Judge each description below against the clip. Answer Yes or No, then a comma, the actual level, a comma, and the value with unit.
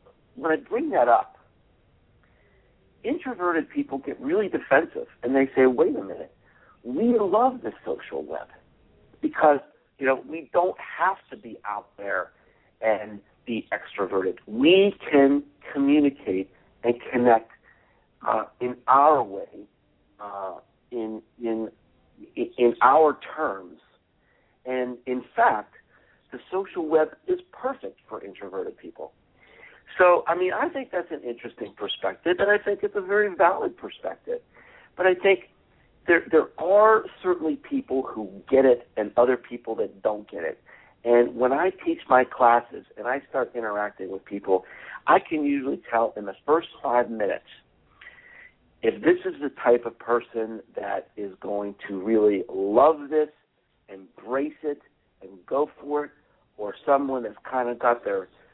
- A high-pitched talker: No, medium, 140 Hz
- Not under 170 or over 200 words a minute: No, average, 145 wpm